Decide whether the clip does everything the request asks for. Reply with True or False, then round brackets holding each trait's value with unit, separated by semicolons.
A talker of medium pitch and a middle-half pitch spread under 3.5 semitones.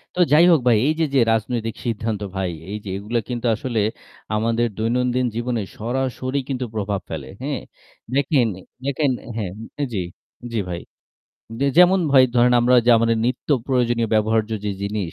False (120 Hz; 3.0 semitones)